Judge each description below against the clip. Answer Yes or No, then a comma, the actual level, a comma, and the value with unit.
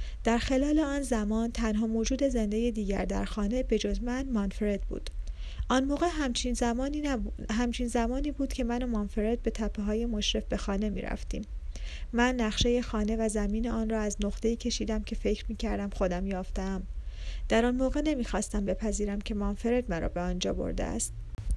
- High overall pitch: Yes, high, 225 Hz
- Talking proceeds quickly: Yes, fast, 180 wpm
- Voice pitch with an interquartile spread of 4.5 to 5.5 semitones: No, average, 2.8 semitones